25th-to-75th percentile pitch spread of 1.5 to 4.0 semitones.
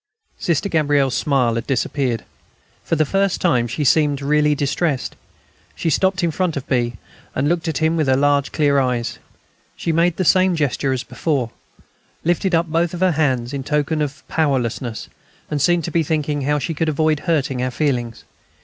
Yes: average, 3.6 semitones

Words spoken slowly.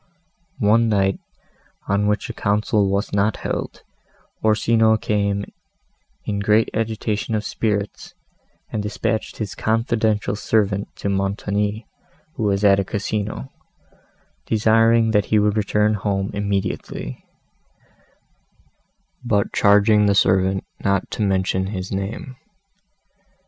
Yes: slow, 110 wpm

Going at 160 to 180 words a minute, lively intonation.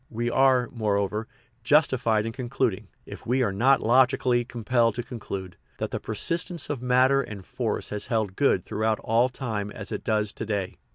No: average, 175 wpm; average, 3.2 semitones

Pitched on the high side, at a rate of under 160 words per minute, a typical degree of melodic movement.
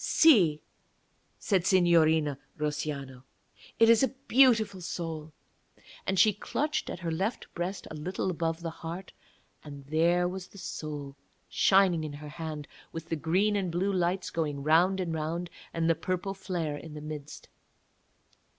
No: medium, 170 Hz; average, 150 wpm; average, 3.6 semitones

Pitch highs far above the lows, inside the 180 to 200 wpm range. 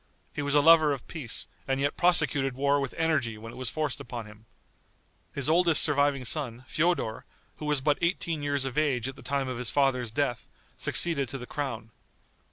No: average, 3.3 semitones; average, 195 wpm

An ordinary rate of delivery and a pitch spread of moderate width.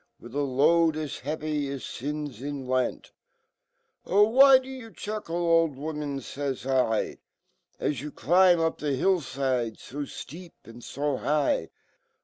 No: slow, 125 wpm; average, 3.7 semitones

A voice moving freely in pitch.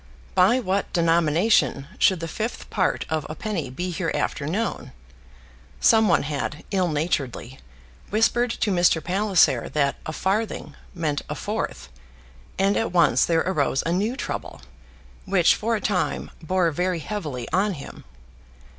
No: average, 4.7 semitones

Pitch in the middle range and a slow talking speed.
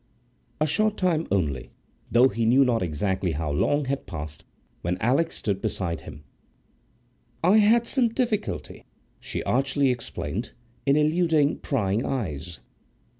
No: low, 125 Hz; slow, 125 wpm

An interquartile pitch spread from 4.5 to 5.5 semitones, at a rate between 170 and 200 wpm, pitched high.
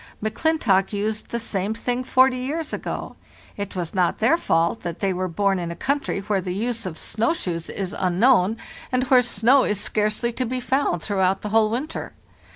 Yes: average, 5.0 semitones; average, 190 wpm; high, 215 Hz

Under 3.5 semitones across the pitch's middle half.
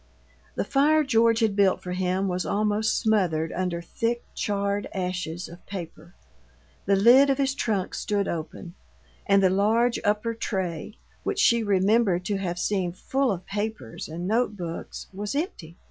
No: average, 3.8 semitones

